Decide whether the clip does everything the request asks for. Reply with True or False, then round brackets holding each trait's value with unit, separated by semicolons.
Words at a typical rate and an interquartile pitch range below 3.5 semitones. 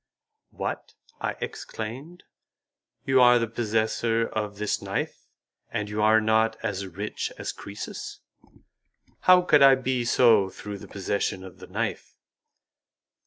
False (130 wpm; 2.9 semitones)